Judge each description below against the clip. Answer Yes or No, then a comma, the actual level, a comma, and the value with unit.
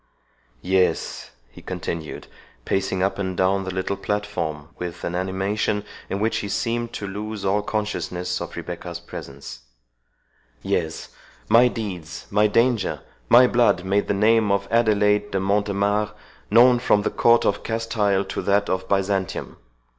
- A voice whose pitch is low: Yes, low, 100 Hz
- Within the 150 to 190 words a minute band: No, average, 140 wpm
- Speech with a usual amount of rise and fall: No, narrow, 2.3 semitones